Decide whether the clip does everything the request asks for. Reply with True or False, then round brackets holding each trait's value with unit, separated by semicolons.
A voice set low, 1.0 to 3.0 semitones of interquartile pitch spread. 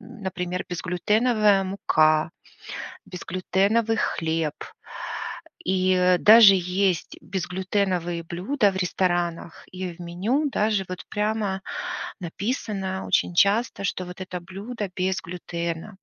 False (185 Hz; 2.5 semitones)